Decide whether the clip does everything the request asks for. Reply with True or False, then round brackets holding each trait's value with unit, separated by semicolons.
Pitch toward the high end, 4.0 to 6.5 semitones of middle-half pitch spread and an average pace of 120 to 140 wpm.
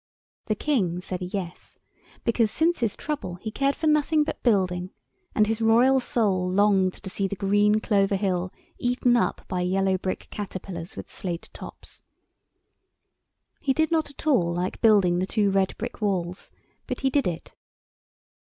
False (200 Hz; 4.8 semitones; 160 wpm)